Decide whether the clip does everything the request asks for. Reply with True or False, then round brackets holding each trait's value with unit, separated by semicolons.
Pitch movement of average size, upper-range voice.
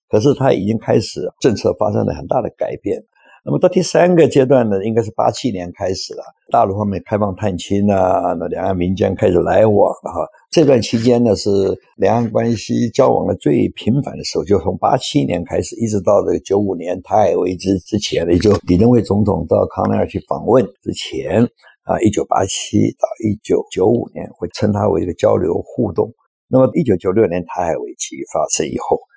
False (4.3 semitones; 105 Hz)